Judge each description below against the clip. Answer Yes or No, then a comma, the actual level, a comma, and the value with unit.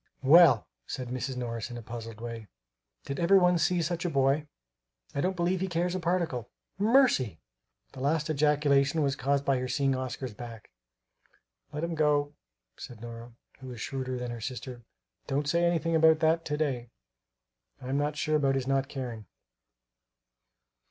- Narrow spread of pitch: No, average, 4.5 semitones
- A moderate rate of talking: Yes, average, 165 wpm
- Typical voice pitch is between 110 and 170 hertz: Yes, medium, 140 Hz